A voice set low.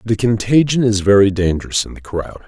Yes: low, 105 Hz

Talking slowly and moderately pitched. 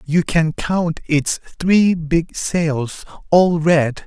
Yes: slow, 120 wpm; medium, 165 Hz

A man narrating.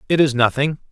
Yes: male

